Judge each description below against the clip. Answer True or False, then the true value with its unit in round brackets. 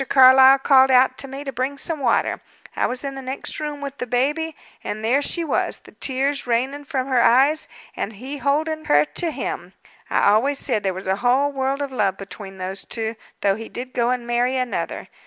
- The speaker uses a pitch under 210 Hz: False (260 Hz)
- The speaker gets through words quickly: True (210 wpm)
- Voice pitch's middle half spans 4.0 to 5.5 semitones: False (3.1 semitones)